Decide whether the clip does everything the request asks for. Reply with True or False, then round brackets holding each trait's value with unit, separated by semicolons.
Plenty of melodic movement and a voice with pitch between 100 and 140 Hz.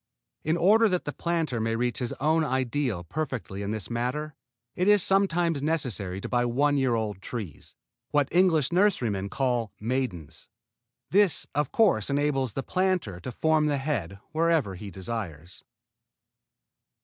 True (6.6 semitones; 135 Hz)